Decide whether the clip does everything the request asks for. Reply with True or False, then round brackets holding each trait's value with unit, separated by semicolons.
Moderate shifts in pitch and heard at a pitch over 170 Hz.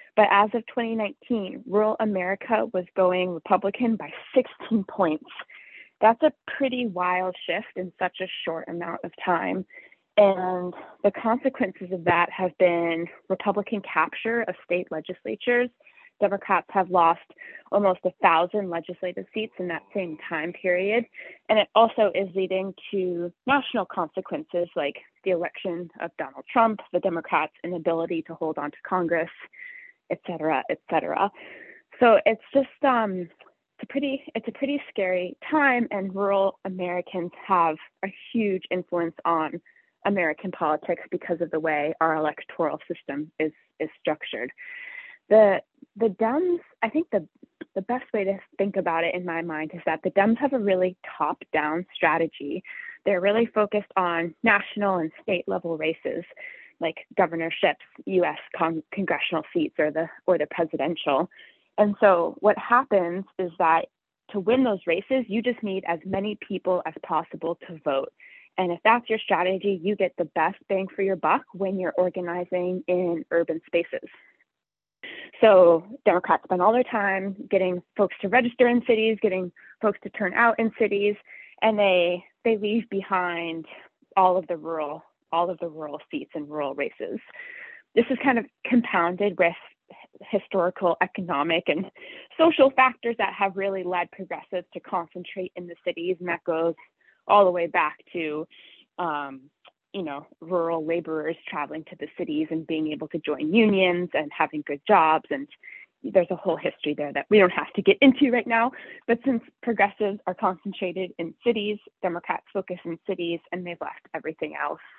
True (4.6 semitones; 190 Hz)